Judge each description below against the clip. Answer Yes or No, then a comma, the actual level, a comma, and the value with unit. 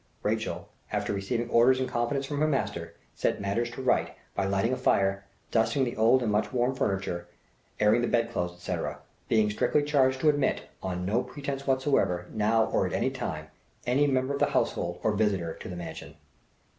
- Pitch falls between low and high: No, low, 115 Hz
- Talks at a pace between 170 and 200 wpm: Yes, average, 190 wpm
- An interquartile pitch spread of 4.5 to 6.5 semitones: Yes, average, 5.0 semitones